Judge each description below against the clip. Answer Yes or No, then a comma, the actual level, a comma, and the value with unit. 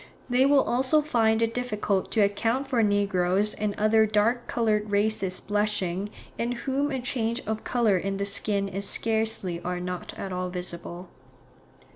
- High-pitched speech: Yes, high, 210 Hz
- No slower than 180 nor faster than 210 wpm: No, average, 160 wpm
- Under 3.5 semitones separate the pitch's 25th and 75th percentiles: Yes, average, 3.1 semitones